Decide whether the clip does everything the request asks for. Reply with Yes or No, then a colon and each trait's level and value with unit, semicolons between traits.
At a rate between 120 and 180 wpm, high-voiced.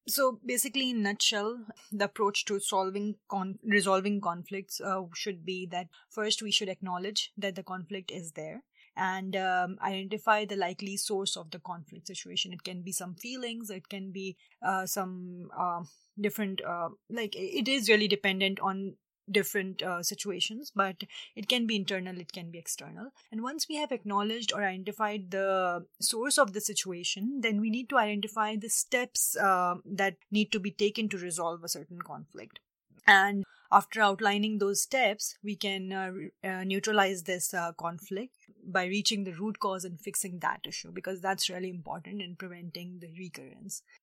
Yes: average, 170 wpm; high, 195 Hz